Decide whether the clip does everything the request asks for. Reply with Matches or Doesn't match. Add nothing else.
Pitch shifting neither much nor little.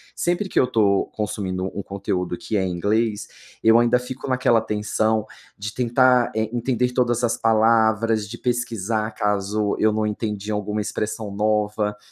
Doesn't match